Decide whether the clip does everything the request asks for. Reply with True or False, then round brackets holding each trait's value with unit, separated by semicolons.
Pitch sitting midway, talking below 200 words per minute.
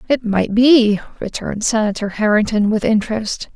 False (220 Hz; 135 wpm)